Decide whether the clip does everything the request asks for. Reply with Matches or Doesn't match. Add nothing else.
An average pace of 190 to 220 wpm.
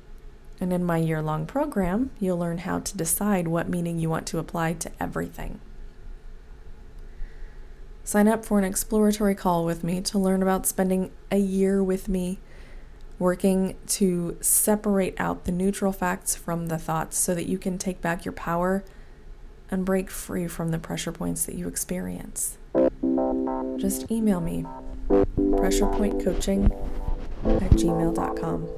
Doesn't match